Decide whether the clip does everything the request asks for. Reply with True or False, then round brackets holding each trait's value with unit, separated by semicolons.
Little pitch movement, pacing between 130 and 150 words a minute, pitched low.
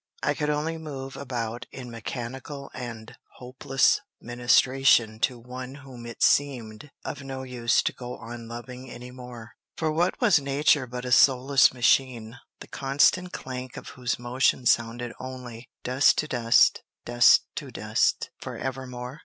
True (2.1 semitones; 145 wpm; 125 Hz)